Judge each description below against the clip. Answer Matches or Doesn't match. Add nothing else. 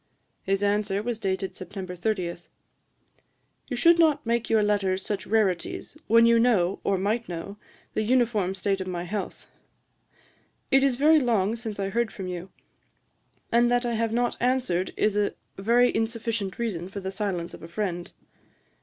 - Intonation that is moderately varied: Matches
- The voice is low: Doesn't match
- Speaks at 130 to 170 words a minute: Matches